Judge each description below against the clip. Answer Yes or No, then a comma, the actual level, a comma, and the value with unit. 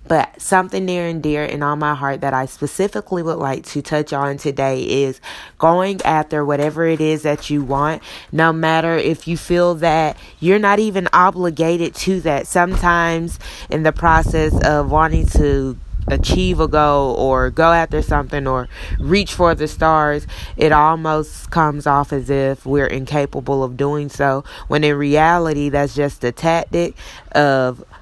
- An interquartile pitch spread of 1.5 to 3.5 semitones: Yes, average, 2.8 semitones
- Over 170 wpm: No, average, 165 wpm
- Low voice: No, medium, 150 Hz